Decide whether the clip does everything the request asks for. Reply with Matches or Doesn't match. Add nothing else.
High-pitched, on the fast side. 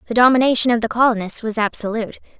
Doesn't match